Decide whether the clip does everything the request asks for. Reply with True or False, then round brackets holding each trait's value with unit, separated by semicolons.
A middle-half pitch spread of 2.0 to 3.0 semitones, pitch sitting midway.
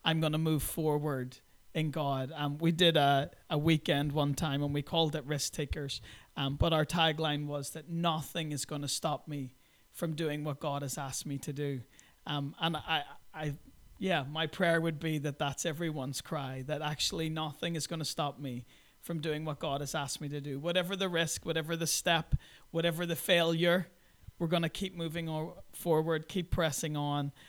True (2.4 semitones; 155 Hz)